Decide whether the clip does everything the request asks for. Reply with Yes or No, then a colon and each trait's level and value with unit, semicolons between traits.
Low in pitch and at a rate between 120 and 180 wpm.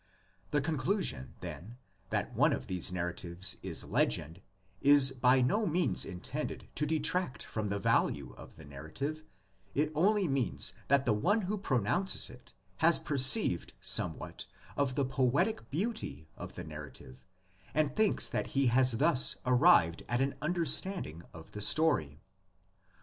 Yes: low, 130 Hz; average, 145 wpm